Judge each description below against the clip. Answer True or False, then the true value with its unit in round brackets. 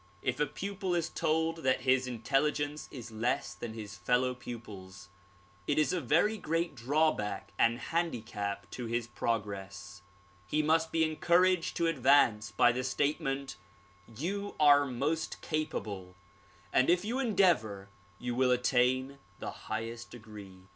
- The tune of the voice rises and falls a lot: True (6.1 semitones)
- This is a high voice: False (130 Hz)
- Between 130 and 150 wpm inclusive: True (140 wpm)